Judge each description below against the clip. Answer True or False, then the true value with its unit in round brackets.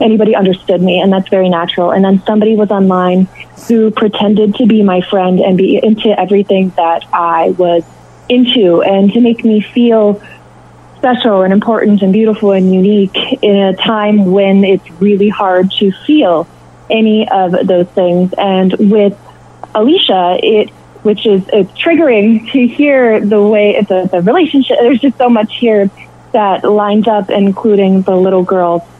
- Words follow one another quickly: False (165 wpm)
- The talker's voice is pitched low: False (205 Hz)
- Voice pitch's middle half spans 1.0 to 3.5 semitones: True (2.6 semitones)